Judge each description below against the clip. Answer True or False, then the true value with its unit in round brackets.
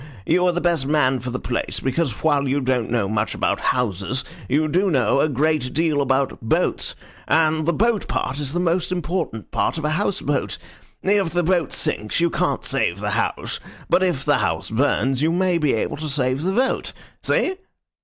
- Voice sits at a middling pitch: True (150 Hz)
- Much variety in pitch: False (4.9 semitones)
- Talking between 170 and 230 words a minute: True (200 wpm)